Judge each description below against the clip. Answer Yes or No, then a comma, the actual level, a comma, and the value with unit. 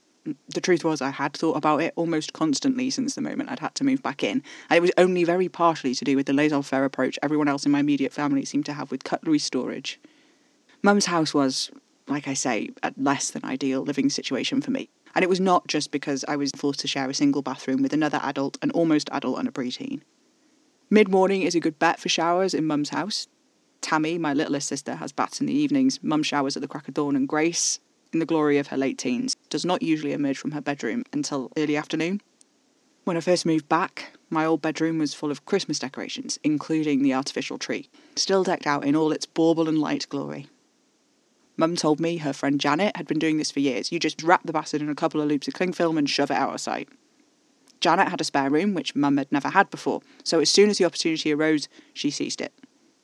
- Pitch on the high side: No, medium, 160 Hz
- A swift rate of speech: Yes, fast, 235 wpm